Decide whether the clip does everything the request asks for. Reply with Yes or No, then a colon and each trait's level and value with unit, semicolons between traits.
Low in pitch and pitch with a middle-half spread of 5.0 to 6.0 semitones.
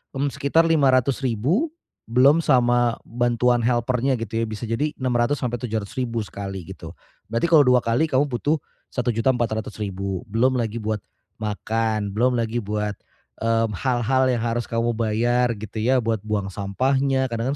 No: low, 120 Hz; average, 2.7 semitones